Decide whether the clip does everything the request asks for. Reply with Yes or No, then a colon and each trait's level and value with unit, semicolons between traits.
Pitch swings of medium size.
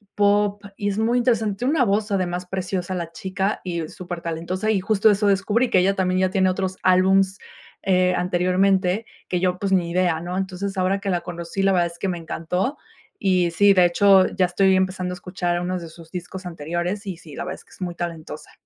No: narrow, 1.9 semitones